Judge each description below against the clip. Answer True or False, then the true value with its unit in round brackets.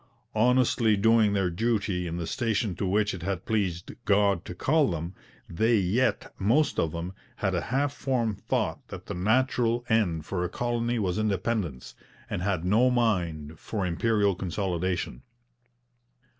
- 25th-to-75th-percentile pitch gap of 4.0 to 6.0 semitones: True (4.5 semitones)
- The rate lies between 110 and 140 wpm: False (155 wpm)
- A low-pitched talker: True (100 Hz)